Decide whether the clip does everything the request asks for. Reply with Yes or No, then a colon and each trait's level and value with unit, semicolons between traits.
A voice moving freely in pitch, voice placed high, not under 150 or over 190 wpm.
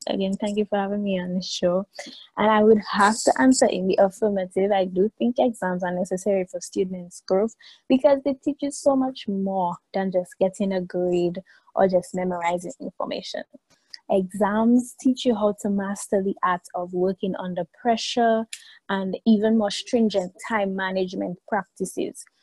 No: average, 3.2 semitones; high, 200 Hz; average, 165 wpm